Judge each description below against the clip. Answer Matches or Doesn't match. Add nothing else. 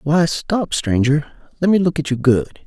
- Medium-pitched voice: Matches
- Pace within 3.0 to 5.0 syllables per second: Matches